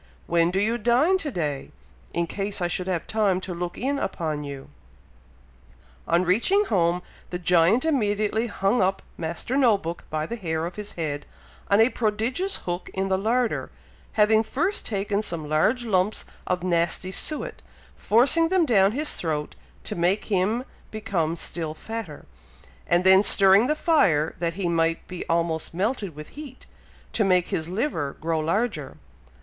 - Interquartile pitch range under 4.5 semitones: No, average, 5.1 semitones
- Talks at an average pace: Yes, average, 165 wpm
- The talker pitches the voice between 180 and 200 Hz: Yes, high, 190 Hz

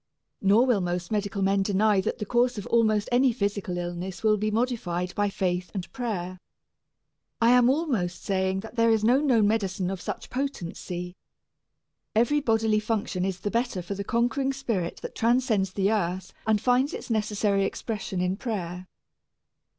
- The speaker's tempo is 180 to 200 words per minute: No, average, 165 wpm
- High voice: Yes, high, 210 Hz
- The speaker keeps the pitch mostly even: No, average, 3.8 semitones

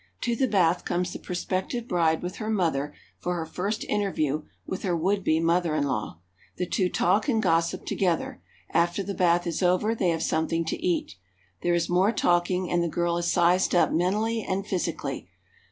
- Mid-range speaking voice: Yes, medium, 175 Hz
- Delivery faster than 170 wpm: Yes, average, 195 wpm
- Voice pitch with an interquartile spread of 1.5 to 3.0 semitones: Yes, narrow, 2.4 semitones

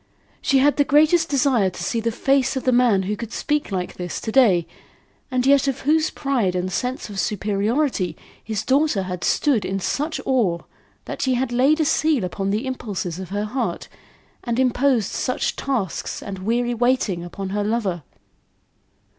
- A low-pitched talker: No, high, 235 Hz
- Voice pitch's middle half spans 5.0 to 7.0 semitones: Yes, wide, 5.6 semitones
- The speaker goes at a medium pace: Yes, average, 180 wpm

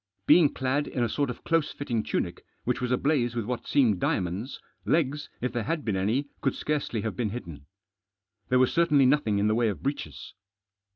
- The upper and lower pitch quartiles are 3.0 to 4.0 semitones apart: No, average, 4.8 semitones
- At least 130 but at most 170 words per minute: No, average, 195 wpm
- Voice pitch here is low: Yes, low, 125 Hz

